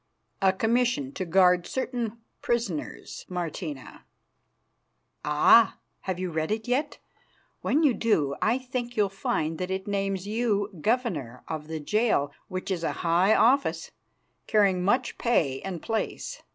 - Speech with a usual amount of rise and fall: No, wide, 5.7 semitones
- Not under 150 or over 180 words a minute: No, average, 140 wpm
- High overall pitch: Yes, high, 195 Hz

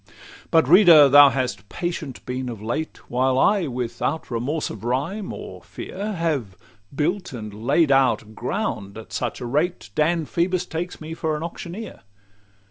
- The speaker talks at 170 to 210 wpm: No, average, 160 wpm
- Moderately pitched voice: Yes, medium, 150 Hz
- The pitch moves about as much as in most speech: No, wide, 5.7 semitones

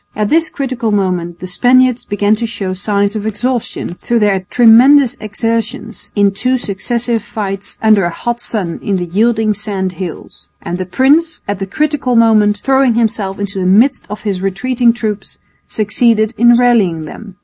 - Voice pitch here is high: Yes, high, 215 Hz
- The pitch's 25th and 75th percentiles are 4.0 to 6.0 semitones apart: No, average, 3.5 semitones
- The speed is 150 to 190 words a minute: Yes, average, 170 wpm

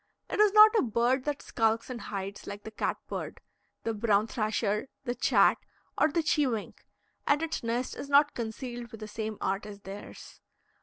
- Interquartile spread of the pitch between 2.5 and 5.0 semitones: Yes, average, 4.6 semitones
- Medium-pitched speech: No, high, 230 Hz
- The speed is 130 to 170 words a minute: No, average, 185 wpm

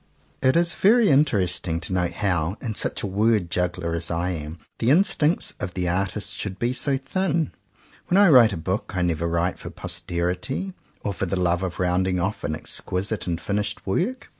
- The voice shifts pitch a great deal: Yes, wide, 5.8 semitones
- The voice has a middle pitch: No, very low, 95 Hz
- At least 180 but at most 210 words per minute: Yes, average, 190 wpm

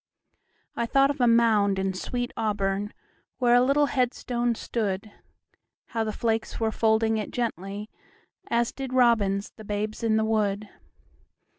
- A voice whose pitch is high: Yes, high, 220 Hz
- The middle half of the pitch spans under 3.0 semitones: Yes, narrow, 2.6 semitones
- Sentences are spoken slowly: Yes, slow, 130 wpm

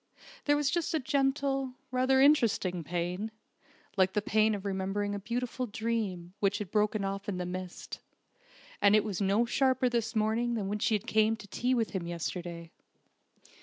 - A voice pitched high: Yes, high, 215 Hz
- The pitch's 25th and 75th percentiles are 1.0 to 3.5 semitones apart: No, average, 4.2 semitones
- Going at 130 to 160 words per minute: No, average, 170 wpm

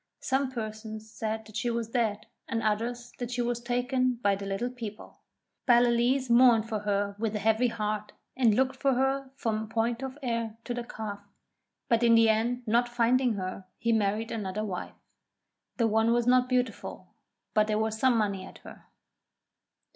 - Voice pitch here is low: No, high, 230 Hz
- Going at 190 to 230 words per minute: No, average, 175 wpm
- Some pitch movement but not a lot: No, narrow, 2.3 semitones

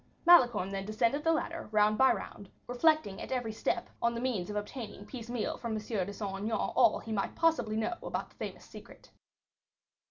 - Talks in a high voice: Yes, high, 225 Hz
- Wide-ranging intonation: No, average, 3.6 semitones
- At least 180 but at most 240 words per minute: Yes, average, 190 wpm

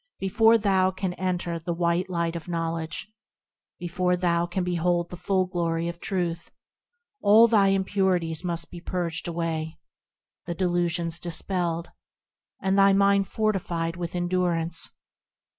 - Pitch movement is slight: Yes, narrow, 1.9 semitones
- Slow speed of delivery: Yes, slow, 130 wpm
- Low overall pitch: No, medium, 175 Hz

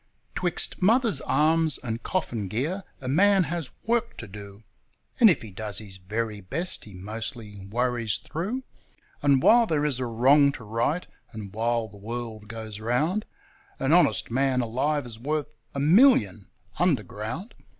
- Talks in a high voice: No, low, 125 Hz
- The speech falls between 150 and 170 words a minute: Yes, average, 155 wpm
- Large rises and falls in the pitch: Yes, wide, 6.8 semitones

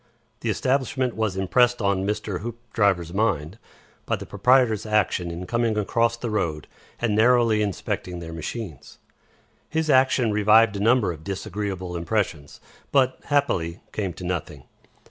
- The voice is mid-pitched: No, low, 105 Hz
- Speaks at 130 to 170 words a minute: Yes, average, 140 wpm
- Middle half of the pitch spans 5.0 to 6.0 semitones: No, average, 4.6 semitones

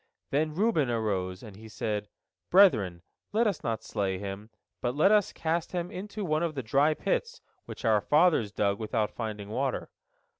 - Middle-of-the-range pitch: No, low, 125 Hz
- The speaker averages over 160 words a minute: Yes, average, 175 wpm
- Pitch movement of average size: No, wide, 8.4 semitones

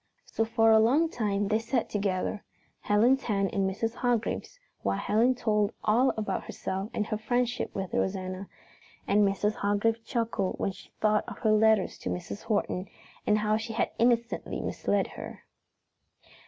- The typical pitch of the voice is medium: No, high, 215 Hz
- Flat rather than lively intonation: Yes, narrow, 2.3 semitones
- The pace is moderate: Yes, average, 160 wpm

